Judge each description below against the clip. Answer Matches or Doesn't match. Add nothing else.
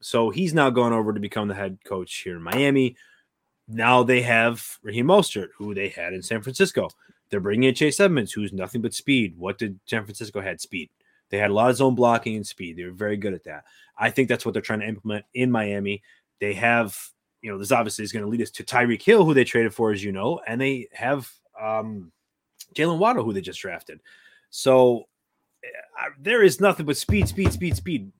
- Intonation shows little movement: Doesn't match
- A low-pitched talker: Matches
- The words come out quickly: Matches